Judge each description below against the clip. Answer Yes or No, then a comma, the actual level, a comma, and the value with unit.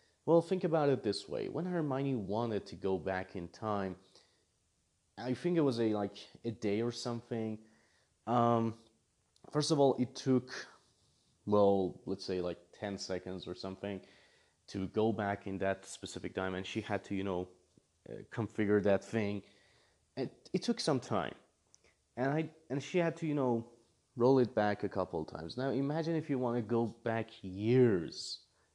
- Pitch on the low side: Yes, low, 110 Hz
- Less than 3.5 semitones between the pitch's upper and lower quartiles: No, average, 5.0 semitones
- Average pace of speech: Yes, average, 175 wpm